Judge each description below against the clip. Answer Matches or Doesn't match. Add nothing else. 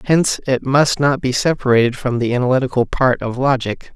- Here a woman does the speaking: Doesn't match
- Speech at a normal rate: Matches